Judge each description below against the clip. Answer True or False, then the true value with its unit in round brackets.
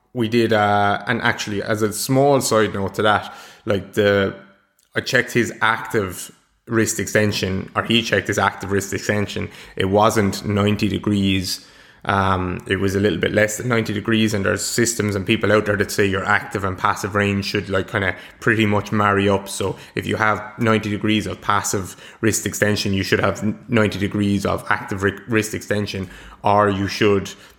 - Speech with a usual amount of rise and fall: False (1.5 semitones)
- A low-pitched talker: True (105 Hz)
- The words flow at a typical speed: True (185 wpm)